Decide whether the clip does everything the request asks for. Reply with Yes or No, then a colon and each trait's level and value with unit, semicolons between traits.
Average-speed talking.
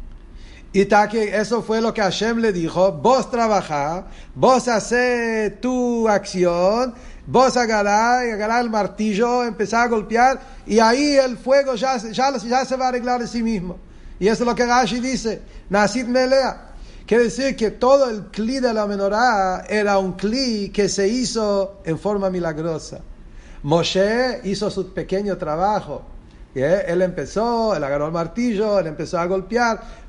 Yes: average, 160 wpm